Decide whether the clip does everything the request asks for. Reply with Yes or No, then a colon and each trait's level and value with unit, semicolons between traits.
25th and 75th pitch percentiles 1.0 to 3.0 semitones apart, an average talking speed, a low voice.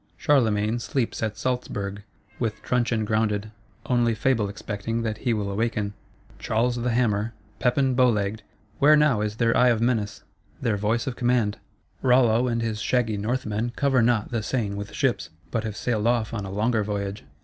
Yes: average, 2.7 semitones; average, 170 wpm; low, 115 Hz